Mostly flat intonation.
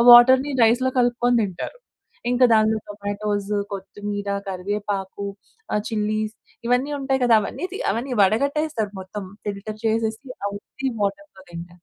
No: average, 3.4 semitones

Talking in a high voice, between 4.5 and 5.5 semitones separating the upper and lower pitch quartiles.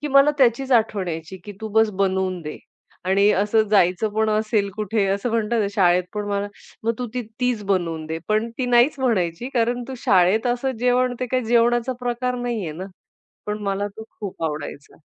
No: high, 215 Hz; average, 3.9 semitones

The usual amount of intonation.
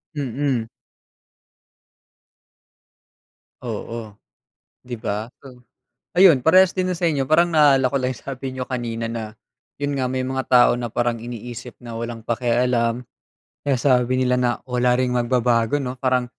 No: narrow, 2.1 semitones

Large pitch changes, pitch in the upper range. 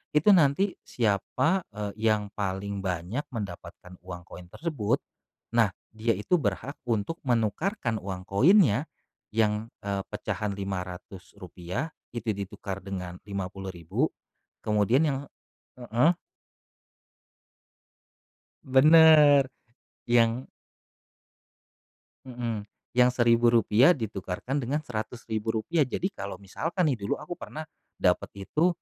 No: wide, 5.7 semitones; low, 110 Hz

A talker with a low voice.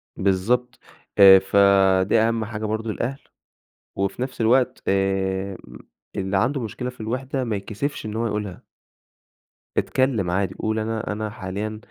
Yes: low, 110 Hz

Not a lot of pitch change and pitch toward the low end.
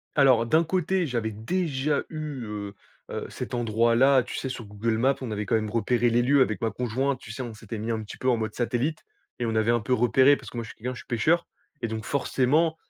No: average, 3.6 semitones; low, 120 Hz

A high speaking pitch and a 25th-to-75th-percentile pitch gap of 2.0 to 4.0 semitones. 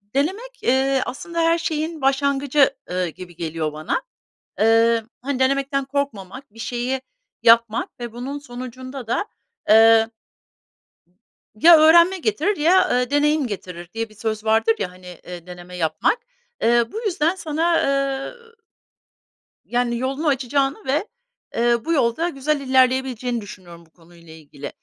No: very high, 255 Hz; average, 4.7 semitones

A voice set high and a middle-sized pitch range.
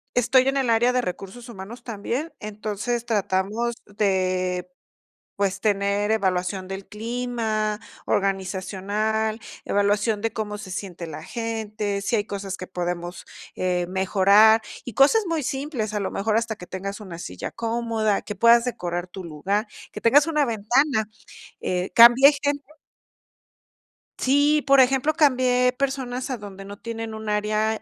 Yes: high, 215 Hz; average, 3.6 semitones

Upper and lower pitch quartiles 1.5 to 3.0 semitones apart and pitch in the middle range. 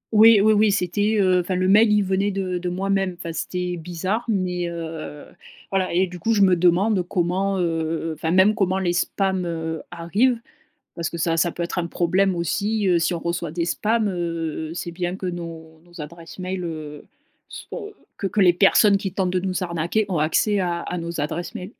Yes: narrow, 2.5 semitones; medium, 180 Hz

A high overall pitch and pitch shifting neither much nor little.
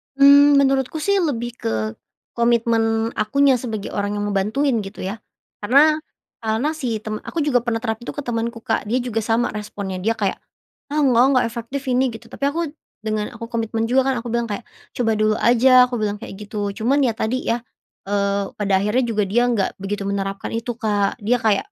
Yes: high, 230 Hz; average, 3.1 semitones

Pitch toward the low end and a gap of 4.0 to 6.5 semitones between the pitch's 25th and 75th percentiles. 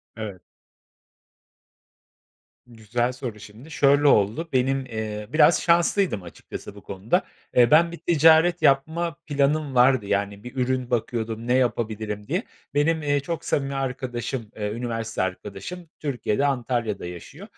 Yes: low, 125 Hz; average, 5.2 semitones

